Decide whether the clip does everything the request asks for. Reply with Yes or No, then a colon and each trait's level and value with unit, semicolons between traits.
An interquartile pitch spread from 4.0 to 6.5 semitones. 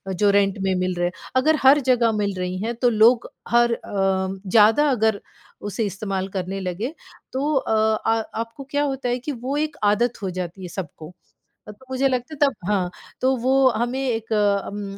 Yes: average, 4.7 semitones